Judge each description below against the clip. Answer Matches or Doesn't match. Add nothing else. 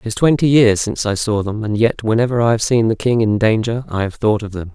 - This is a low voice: Matches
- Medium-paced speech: Doesn't match